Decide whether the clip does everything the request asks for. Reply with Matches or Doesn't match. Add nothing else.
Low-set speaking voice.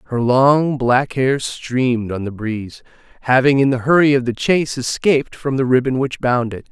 Matches